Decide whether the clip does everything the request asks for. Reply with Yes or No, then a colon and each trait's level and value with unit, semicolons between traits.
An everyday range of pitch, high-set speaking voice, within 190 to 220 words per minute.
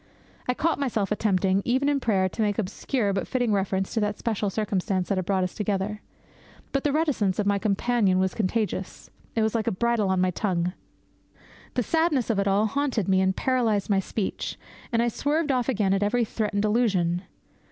Yes: average, 3.8 semitones; high, 210 Hz; average, 195 wpm